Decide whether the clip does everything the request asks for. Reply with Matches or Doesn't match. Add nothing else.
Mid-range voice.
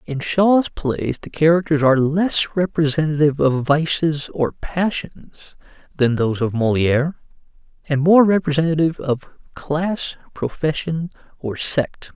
Matches